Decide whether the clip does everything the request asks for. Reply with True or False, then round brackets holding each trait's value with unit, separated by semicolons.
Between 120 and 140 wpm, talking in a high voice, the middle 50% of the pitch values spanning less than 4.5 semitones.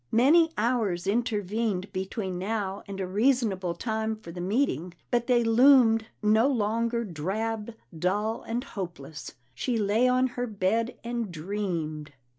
True (135 wpm; 215 Hz; 3.9 semitones)